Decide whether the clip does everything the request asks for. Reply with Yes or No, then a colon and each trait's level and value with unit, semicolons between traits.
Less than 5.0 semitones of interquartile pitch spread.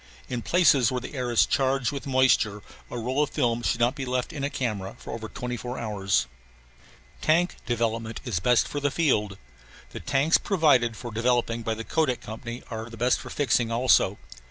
Yes: average, 2.9 semitones